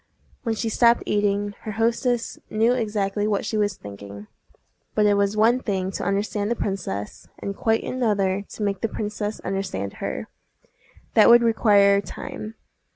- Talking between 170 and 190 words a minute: No, average, 160 wpm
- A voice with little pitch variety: Yes, narrow, 2.2 semitones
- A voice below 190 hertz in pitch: No, high, 205 Hz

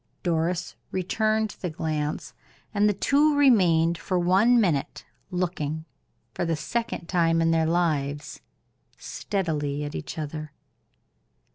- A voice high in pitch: No, medium, 170 Hz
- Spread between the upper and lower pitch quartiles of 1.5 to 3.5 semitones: No, average, 3.9 semitones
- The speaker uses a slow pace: Yes, slow, 120 wpm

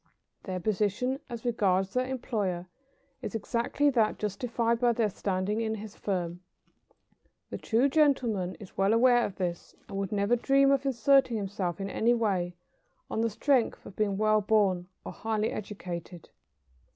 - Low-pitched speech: No, high, 215 Hz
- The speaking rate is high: No, average, 155 wpm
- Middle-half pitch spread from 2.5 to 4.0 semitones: Yes, average, 3.7 semitones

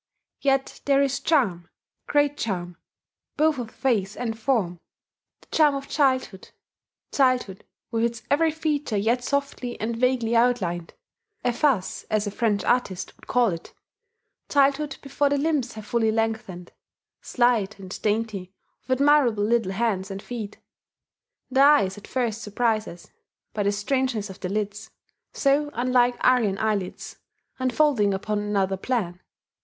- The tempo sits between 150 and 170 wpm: No, average, 140 wpm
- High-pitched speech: Yes, high, 230 Hz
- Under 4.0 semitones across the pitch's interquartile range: No, average, 4.6 semitones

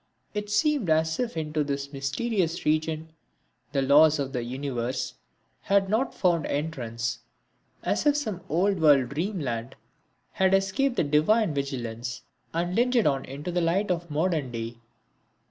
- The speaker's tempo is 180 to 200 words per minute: No, average, 145 wpm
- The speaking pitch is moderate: Yes, medium, 160 Hz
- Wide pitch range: Yes, wide, 5.8 semitones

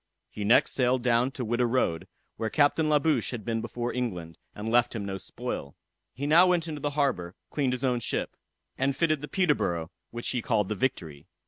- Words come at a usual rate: No, fast, 210 wpm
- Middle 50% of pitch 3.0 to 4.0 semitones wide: No, average, 5.2 semitones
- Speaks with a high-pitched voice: No, low, 120 Hz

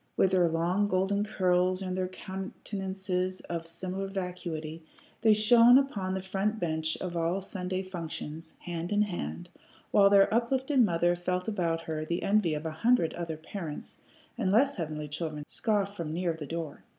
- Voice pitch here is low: No, medium, 185 Hz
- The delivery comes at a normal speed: Yes, average, 170 wpm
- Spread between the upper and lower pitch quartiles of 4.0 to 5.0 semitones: No, average, 3.2 semitones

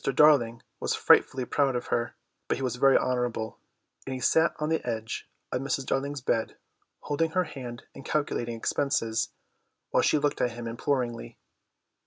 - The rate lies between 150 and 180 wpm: Yes, average, 165 wpm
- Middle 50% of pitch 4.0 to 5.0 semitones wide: No, average, 3.3 semitones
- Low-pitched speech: Yes, low, 130 Hz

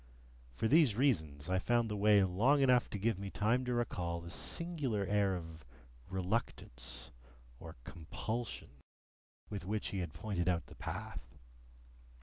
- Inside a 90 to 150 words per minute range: Yes, average, 145 wpm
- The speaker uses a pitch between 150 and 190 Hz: No, low, 100 Hz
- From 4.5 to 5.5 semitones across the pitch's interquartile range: Yes, average, 5.2 semitones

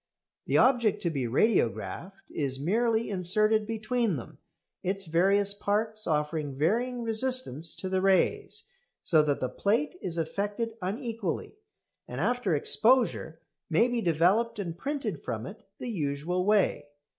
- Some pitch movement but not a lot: No, wide, 5.8 semitones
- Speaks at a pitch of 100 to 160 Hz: No, high, 195 Hz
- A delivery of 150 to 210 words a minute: No, slow, 135 wpm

